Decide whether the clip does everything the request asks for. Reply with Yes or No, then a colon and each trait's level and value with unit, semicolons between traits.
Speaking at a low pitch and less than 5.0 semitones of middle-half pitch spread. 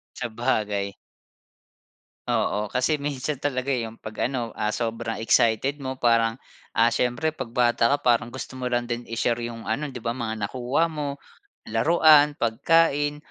Yes: low, 120 Hz; average, 3.5 semitones